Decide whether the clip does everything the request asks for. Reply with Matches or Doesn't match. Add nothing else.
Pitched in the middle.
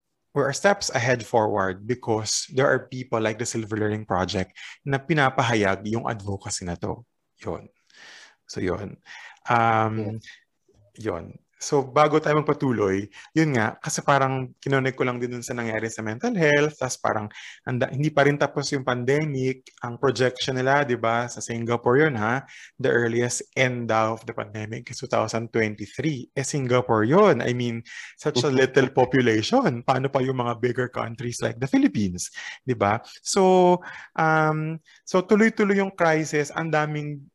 Doesn't match